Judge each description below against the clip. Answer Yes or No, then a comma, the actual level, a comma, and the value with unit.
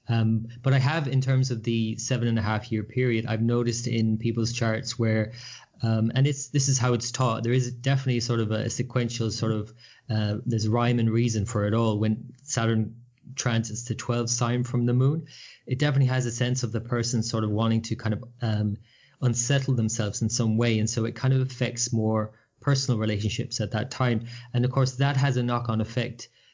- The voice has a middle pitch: No, low, 120 Hz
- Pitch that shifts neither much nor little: No, narrow, 2.1 semitones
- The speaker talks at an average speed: No, fast, 215 wpm